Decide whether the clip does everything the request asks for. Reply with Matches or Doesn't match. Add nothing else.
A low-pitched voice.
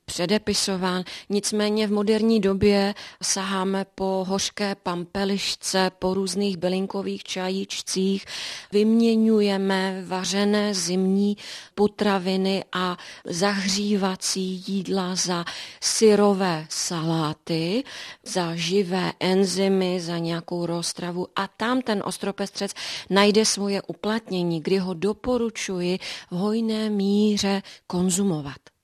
Doesn't match